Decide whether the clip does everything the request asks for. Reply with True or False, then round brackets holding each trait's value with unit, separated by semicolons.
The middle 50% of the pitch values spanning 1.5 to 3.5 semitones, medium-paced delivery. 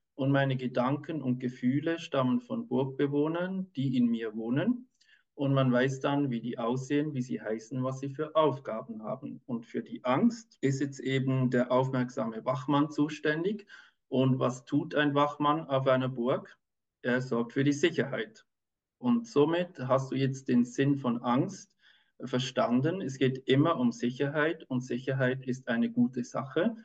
True (3.2 semitones; 160 wpm)